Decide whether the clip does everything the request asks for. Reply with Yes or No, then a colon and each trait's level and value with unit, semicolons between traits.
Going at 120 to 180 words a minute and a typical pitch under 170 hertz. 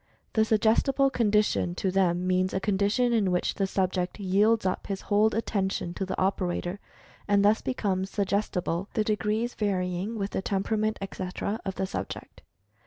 No: average, 160 wpm; high, 200 Hz